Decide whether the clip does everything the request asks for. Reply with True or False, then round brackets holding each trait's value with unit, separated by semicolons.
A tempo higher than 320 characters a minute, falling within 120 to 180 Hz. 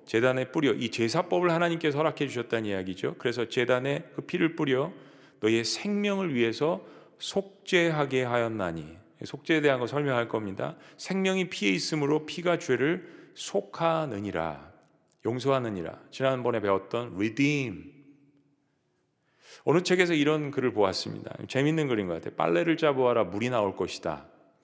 True (340 characters per minute; 140 Hz)